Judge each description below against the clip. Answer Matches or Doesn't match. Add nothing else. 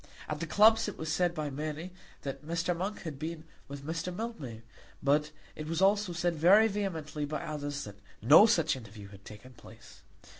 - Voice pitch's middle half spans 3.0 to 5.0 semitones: Matches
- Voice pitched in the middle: Matches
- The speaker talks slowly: Doesn't match